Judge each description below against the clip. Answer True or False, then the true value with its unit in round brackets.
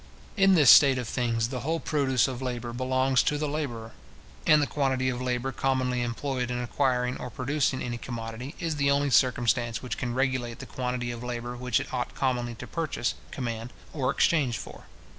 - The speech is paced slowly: False (190 wpm)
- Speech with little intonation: True (2.2 semitones)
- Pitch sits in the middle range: False (125 Hz)